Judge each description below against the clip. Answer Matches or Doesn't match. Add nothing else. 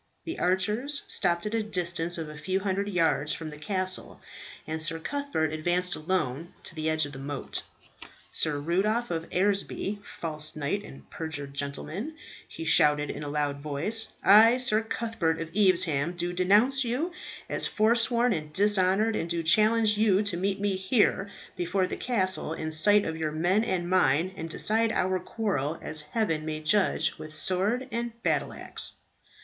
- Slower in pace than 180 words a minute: Matches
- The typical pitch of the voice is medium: Matches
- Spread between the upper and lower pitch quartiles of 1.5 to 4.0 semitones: Doesn't match